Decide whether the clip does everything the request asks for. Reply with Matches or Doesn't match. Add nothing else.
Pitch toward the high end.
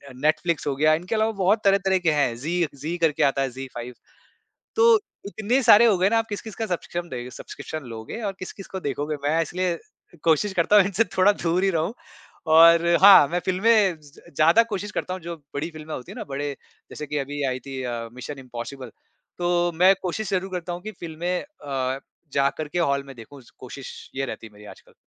Doesn't match